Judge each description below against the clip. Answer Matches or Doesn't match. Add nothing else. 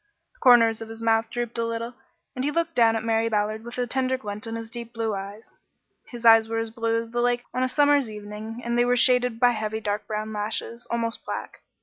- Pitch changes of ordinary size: Doesn't match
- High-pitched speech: Matches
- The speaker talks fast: Matches